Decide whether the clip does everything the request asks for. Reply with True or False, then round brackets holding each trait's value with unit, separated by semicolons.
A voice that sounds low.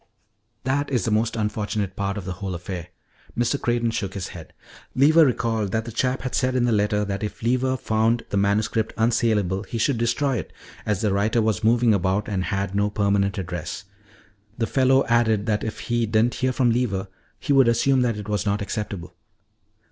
True (110 Hz)